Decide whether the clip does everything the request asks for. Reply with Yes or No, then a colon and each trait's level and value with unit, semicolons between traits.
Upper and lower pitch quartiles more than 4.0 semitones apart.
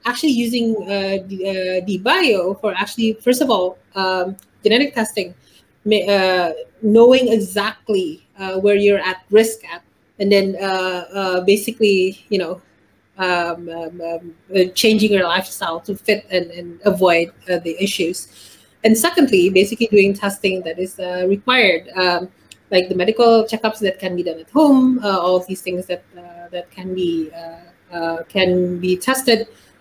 No: average, 3.2 semitones